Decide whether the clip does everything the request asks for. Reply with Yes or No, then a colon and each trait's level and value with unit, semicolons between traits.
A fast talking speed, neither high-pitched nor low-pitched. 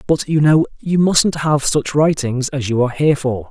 Yes: fast, 225 wpm; medium, 145 Hz